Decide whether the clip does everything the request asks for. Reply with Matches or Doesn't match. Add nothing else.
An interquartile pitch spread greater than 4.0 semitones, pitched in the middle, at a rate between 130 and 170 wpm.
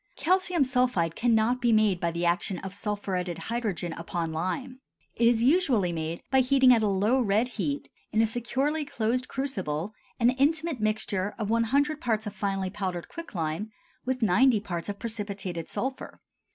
Doesn't match